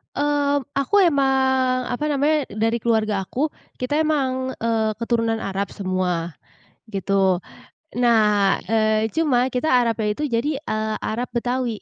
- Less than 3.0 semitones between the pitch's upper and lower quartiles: No, average, 3.4 semitones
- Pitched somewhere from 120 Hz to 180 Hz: No, high, 235 Hz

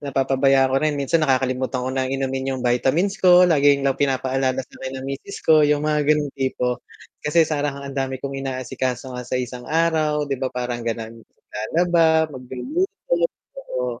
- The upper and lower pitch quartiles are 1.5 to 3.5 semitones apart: Yes, average, 2.8 semitones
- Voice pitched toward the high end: No, low, 135 Hz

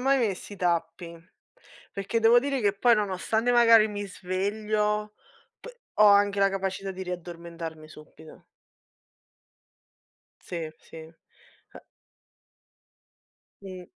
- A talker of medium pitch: No, high, 195 Hz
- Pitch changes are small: No, average, 3.3 semitones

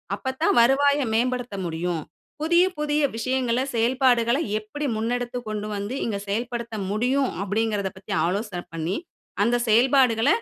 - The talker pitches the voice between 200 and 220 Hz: No, high, 235 Hz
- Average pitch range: Yes, average, 3.8 semitones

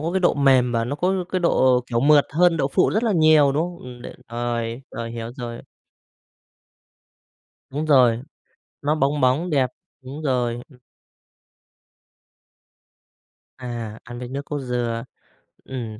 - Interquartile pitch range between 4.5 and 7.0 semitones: No, average, 3.9 semitones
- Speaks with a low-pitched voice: Yes, low, 130 Hz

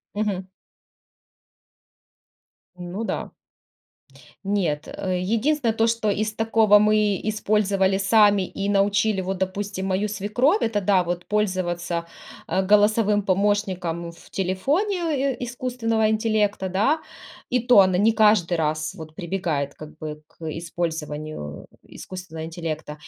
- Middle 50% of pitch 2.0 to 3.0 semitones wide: No, average, 3.5 semitones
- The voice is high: Yes, high, 195 Hz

